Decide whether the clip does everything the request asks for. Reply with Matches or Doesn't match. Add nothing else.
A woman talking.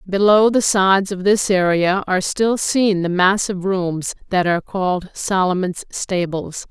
Matches